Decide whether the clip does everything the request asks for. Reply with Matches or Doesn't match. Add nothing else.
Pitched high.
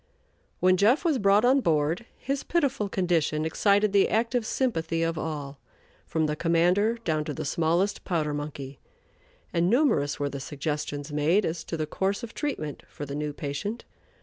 Doesn't match